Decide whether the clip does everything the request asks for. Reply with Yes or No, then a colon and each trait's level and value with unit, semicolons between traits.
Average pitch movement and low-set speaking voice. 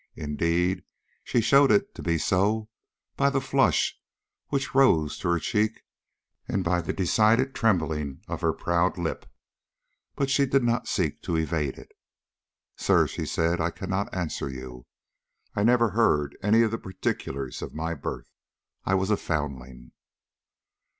No: wide, 6.3 semitones; very low, 90 Hz